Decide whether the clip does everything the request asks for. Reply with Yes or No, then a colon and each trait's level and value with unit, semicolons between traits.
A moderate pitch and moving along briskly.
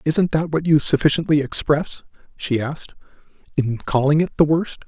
No: medium, 150 Hz; average, 160 wpm